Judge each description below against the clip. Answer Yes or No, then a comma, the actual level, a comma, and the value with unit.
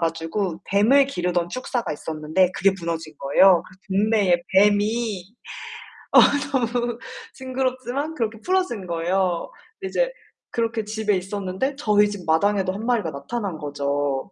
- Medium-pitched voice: No, high, 200 Hz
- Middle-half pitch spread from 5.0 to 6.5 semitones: Yes, wide, 5.4 semitones